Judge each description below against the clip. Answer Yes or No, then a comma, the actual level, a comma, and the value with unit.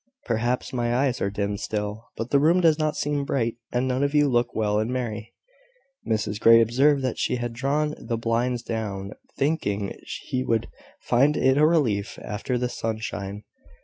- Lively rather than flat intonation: No, average, 3.9 semitones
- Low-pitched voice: Yes, low, 120 Hz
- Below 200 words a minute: Yes, average, 180 wpm